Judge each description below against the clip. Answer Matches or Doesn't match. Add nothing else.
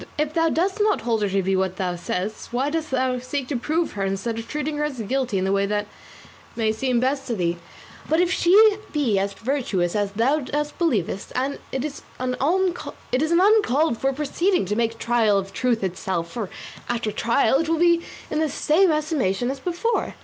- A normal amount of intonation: Doesn't match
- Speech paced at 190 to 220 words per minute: Matches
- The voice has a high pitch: Matches